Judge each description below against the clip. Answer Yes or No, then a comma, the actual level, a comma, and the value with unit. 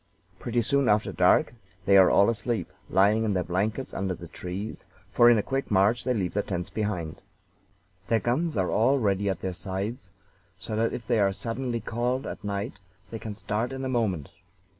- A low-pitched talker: Yes, low, 105 Hz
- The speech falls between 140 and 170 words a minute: No, average, 195 wpm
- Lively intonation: No, average, 3.6 semitones